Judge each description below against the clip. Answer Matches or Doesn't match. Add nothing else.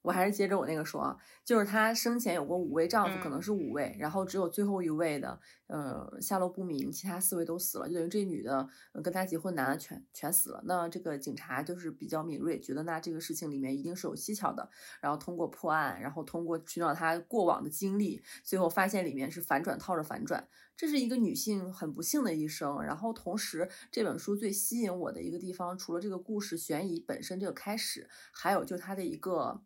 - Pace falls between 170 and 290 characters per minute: Doesn't match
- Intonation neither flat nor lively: Matches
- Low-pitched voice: Doesn't match